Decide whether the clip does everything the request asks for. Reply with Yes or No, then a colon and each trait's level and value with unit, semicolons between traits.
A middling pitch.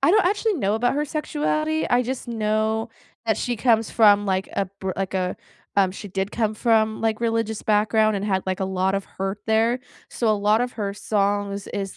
No: high, 215 Hz